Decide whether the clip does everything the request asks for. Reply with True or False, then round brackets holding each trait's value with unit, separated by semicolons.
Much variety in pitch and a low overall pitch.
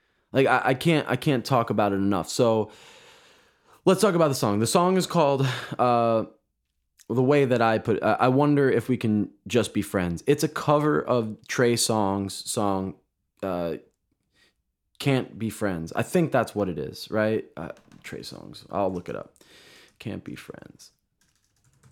True (5.8 semitones; 115 Hz)